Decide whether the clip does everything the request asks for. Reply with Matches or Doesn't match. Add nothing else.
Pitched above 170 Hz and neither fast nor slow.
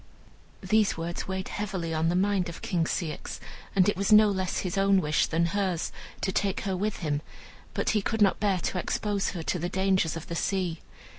Doesn't match